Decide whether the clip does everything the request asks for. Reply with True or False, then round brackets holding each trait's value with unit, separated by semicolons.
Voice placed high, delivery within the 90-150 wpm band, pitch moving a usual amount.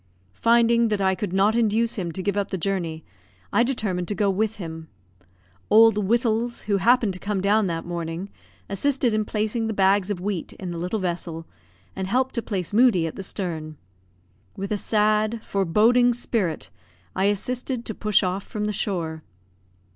False (205 Hz; 175 wpm; 3.4 semitones)